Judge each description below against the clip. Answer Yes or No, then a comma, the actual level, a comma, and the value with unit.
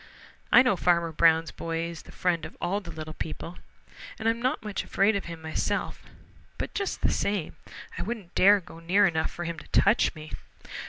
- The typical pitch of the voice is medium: Yes, medium, 175 Hz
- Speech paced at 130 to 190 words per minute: No, average, 200 wpm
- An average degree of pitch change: Yes, average, 3.7 semitones